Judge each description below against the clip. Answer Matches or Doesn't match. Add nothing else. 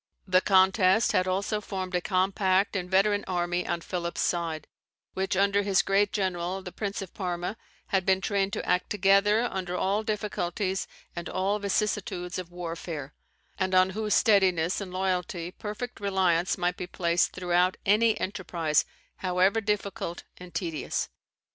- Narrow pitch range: Matches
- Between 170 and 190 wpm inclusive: Doesn't match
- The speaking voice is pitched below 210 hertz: Matches